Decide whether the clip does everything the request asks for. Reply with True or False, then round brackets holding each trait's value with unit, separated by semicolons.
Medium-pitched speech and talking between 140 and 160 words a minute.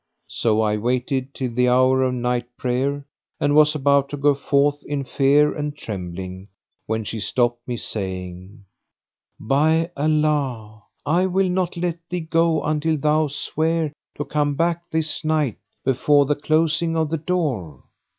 True (145 Hz; 150 wpm)